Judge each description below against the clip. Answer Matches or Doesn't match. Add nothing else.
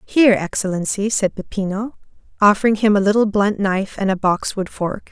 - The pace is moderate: Matches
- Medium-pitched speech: Doesn't match